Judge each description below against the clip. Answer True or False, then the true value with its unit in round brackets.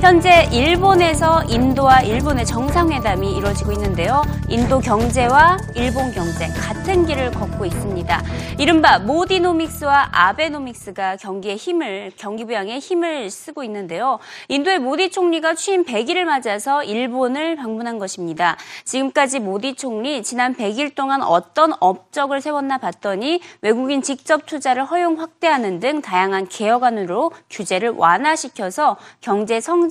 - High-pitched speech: True (275 Hz)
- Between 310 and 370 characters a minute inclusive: True (325 characters per minute)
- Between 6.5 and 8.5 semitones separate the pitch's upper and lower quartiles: True (7.4 semitones)